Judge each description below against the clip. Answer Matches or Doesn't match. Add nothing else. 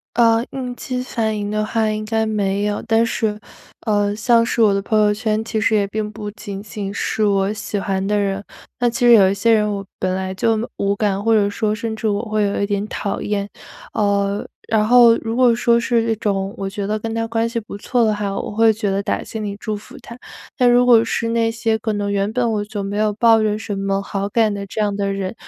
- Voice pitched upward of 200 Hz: Matches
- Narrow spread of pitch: Matches